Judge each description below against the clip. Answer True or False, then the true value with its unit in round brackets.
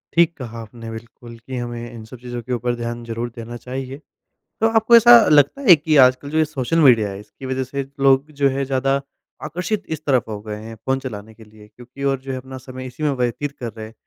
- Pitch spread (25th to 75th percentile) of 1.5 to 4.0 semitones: True (3.0 semitones)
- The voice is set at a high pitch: False (130 Hz)